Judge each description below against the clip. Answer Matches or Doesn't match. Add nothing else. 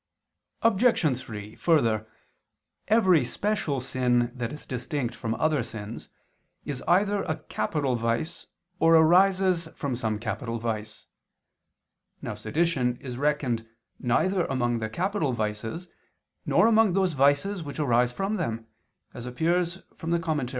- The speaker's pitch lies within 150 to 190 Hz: Doesn't match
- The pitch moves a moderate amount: Doesn't match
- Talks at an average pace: Doesn't match